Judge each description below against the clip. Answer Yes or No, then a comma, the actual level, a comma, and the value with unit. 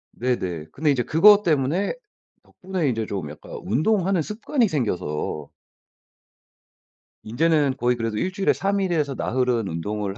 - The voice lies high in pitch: No, low, 135 Hz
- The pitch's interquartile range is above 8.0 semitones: Yes, wide, 9.0 semitones